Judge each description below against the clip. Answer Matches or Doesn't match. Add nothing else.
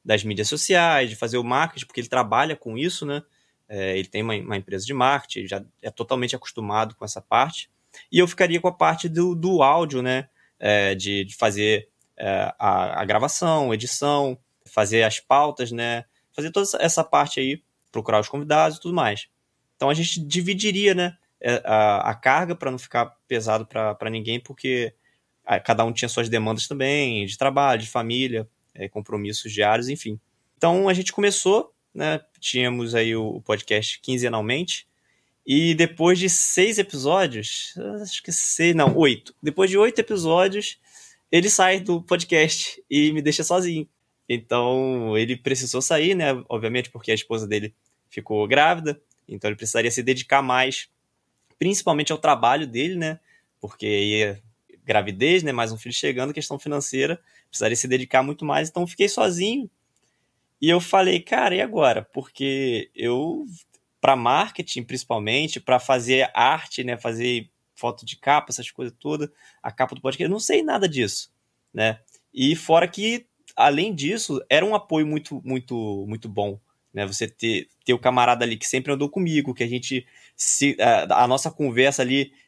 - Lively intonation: Matches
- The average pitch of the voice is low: Matches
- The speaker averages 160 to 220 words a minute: Matches